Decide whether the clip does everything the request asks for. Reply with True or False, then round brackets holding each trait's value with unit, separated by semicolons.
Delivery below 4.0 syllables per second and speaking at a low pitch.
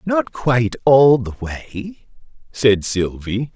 True (3.2 syllables/s; 125 Hz)